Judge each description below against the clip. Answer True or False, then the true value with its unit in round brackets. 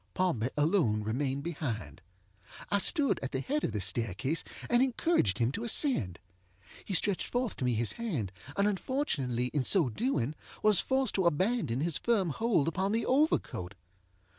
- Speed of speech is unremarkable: True (165 wpm)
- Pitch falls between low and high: True (165 Hz)